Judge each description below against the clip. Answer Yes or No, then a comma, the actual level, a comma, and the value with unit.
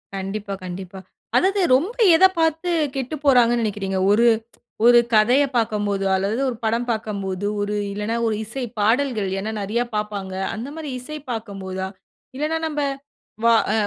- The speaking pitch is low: No, high, 220 Hz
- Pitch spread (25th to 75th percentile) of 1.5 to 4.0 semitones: No, average, 4.6 semitones